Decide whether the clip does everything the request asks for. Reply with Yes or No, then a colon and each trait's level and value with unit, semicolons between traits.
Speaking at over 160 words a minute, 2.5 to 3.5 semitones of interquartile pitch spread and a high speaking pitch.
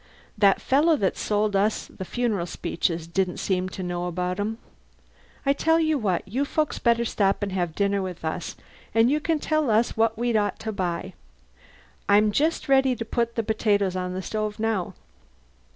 No: average, 185 wpm; average, 4.1 semitones; high, 210 Hz